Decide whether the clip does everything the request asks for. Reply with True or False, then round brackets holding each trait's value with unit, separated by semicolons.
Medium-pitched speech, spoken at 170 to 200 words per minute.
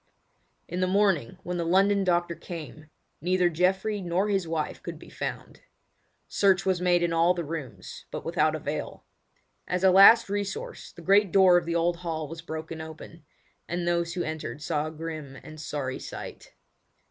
True (175 Hz; 175 wpm)